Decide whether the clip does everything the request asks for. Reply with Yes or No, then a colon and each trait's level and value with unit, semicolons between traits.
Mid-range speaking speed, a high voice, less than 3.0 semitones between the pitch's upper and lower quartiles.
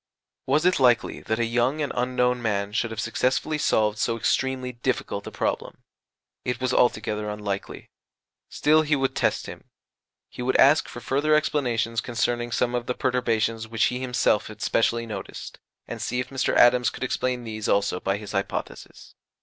No: average, 175 wpm; low, 120 Hz; narrow, 2.6 semitones